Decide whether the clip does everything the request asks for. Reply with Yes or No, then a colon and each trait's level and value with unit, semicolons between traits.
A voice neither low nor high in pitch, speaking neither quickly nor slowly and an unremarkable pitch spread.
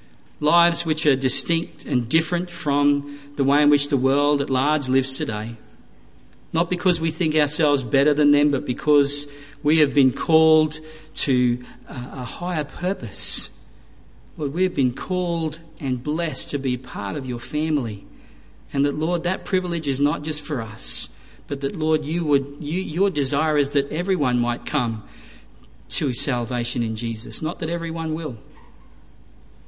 Yes: medium, 145 Hz; average, 160 wpm; average, 3.4 semitones